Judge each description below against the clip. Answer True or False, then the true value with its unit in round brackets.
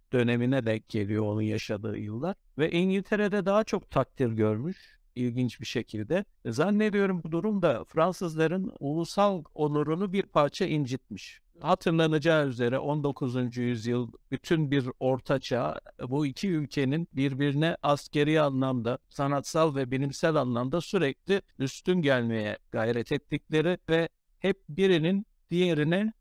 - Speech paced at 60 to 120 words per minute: True (115 wpm)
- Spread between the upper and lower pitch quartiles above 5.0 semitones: True (5.5 semitones)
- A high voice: False (145 Hz)